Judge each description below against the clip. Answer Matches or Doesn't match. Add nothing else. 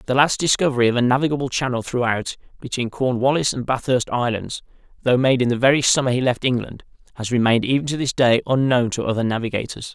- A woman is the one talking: Doesn't match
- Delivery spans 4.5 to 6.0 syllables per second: Doesn't match